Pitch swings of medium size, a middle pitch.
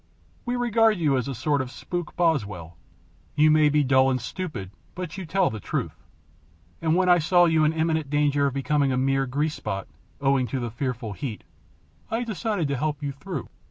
Yes: average, 4.6 semitones; medium, 145 Hz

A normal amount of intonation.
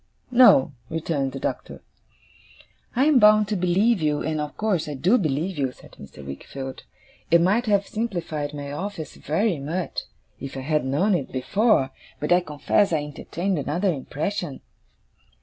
No: wide, 5.8 semitones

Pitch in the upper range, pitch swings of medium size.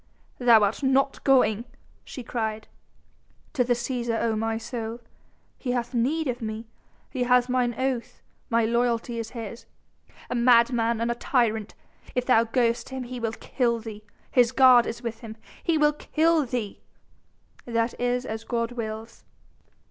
No: high, 235 Hz; narrow, 1.8 semitones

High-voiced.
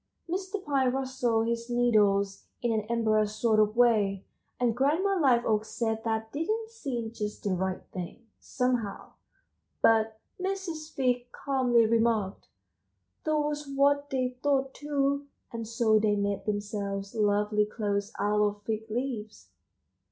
Yes: high, 230 Hz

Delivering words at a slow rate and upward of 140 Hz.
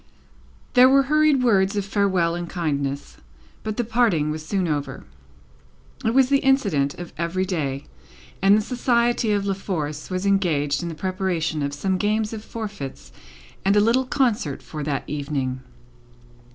No: average, 160 wpm; high, 190 Hz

